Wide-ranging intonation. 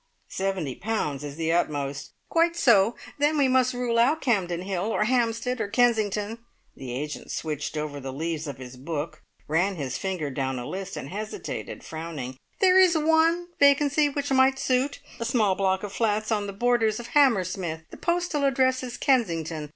Yes: wide, 8.3 semitones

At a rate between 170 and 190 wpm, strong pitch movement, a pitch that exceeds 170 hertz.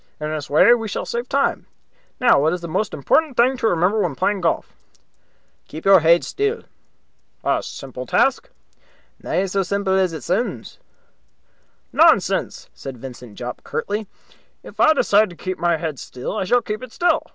Yes: average, 175 wpm; wide, 6.2 semitones; high, 190 Hz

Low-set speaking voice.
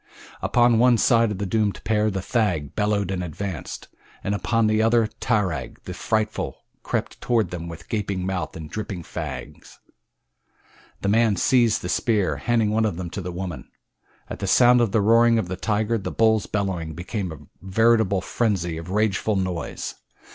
Yes: low, 105 Hz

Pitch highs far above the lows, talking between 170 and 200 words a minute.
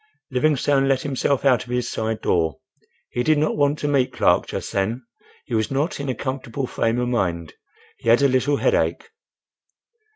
No: average, 3.5 semitones; average, 185 wpm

